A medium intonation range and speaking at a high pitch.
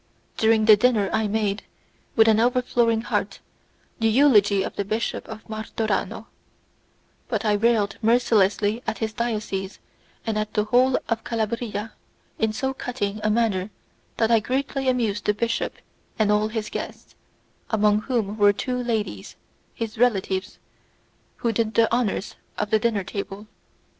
No: narrow, 2.0 semitones; high, 220 Hz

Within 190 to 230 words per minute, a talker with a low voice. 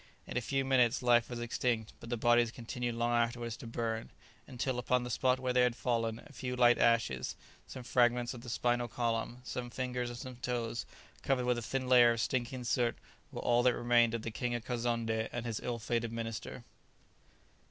Yes: fast, 205 wpm; low, 120 Hz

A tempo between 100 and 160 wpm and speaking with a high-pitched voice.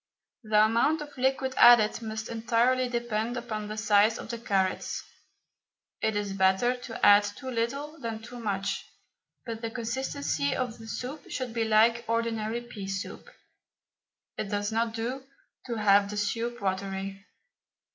Yes: average, 150 wpm; high, 225 Hz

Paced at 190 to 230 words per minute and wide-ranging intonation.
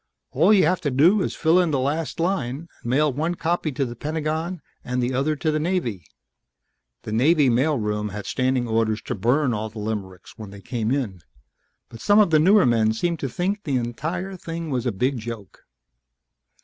Yes: fast, 205 wpm; wide, 6.2 semitones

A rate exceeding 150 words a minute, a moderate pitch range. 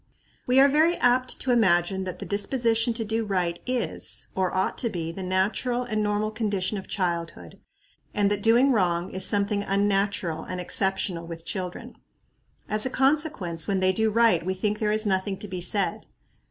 Yes: average, 180 wpm; average, 3.4 semitones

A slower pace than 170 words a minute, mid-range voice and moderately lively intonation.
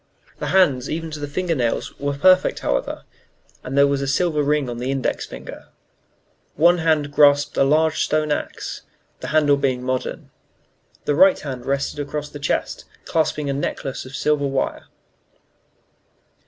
No: average, 160 wpm; medium, 145 Hz; narrow, 2.1 semitones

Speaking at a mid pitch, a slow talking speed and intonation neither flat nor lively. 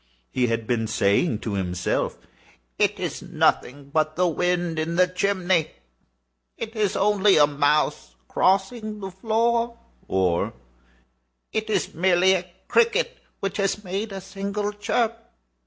No: medium, 180 Hz; slow, 125 wpm; wide, 6.9 semitones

